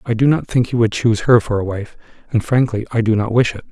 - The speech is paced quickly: Yes, fast, 290 wpm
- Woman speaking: No, male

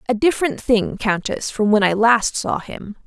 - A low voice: No, high, 220 Hz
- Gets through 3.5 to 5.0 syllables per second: Yes, 4.6 syllables/s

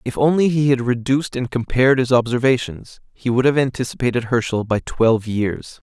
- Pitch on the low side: Yes, low, 125 Hz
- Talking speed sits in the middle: Yes, average, 175 wpm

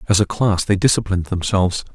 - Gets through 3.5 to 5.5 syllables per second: No, 6.5 syllables/s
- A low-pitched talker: Yes, very low, 95 Hz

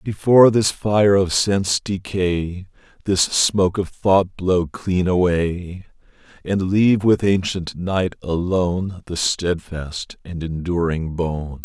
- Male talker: Yes, male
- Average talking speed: No, slow, 125 wpm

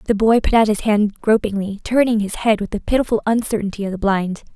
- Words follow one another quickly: Yes, fast, 225 wpm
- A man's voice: No, female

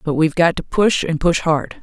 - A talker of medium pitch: Yes, medium, 165 Hz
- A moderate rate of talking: No, fast, 265 wpm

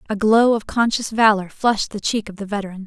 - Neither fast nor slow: No, fast, 230 wpm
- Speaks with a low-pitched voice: No, high, 210 Hz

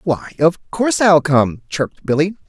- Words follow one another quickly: No, average, 170 wpm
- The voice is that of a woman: No, male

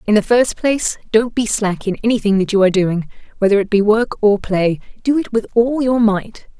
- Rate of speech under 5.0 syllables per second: No, 5.4 syllables/s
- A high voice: Yes, high, 215 Hz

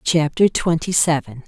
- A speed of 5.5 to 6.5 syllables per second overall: No, 4.4 syllables/s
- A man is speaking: No, female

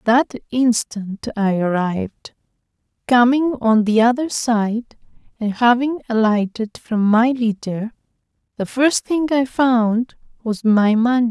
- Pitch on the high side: Yes, high, 230 Hz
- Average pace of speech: No, slow, 120 wpm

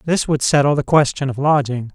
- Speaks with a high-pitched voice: No, medium, 140 Hz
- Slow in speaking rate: No, fast, 215 wpm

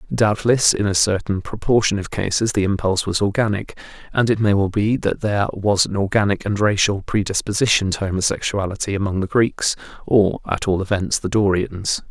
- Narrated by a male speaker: Yes, male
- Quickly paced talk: No, average, 175 wpm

